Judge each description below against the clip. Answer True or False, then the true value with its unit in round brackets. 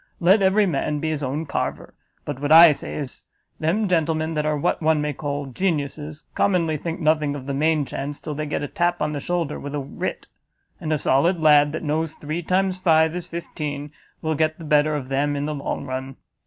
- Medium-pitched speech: True (155 Hz)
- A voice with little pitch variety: True (2.1 semitones)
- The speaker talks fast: True (220 wpm)